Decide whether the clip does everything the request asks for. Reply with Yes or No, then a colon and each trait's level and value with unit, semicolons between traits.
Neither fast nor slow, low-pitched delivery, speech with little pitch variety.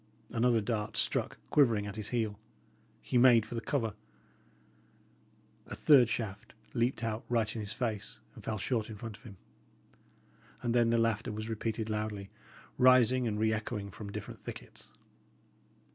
Yes: average, 155 wpm; low, 110 Hz; narrow, 2.0 semitones